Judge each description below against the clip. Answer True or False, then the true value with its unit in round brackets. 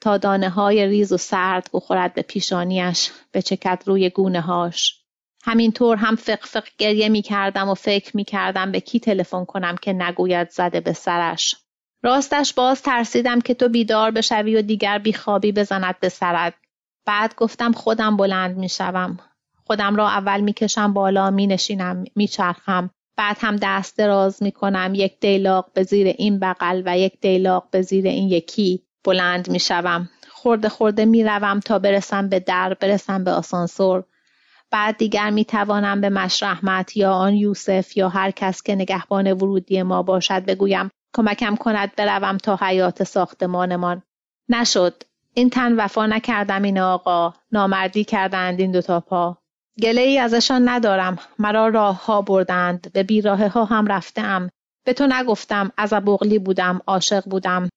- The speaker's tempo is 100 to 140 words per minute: False (155 wpm)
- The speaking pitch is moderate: False (195 Hz)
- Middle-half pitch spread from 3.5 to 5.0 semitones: False (2.4 semitones)